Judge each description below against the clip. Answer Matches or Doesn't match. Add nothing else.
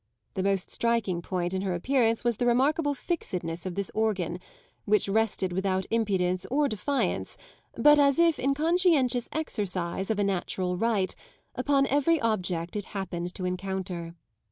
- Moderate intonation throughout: Doesn't match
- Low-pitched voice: Doesn't match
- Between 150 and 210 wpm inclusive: Matches